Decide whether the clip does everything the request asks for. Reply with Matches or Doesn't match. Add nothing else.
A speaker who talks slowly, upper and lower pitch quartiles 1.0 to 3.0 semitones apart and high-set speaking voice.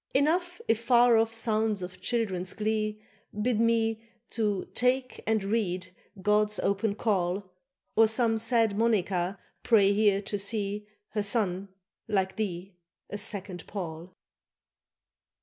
Matches